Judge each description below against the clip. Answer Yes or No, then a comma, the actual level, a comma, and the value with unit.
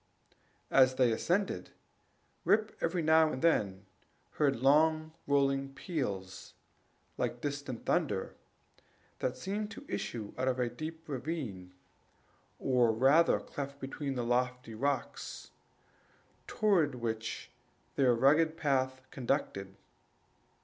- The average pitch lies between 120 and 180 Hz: Yes, low, 135 Hz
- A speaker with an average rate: No, slow, 105 wpm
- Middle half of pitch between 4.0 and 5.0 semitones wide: Yes, average, 4.4 semitones